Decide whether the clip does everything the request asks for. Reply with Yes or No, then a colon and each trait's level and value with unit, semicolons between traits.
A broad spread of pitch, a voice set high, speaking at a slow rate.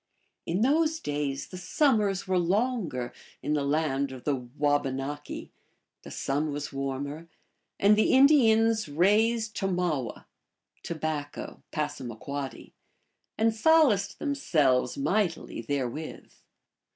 No: wide, 7.4 semitones; medium, 160 Hz; slow, 105 wpm